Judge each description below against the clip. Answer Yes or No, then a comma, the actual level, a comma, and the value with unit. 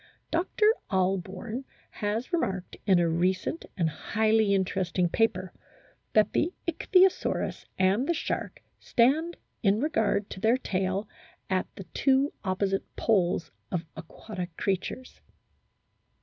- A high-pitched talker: Yes, high, 200 Hz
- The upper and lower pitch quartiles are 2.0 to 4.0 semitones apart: No, average, 5.2 semitones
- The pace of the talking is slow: Yes, slow, 120 wpm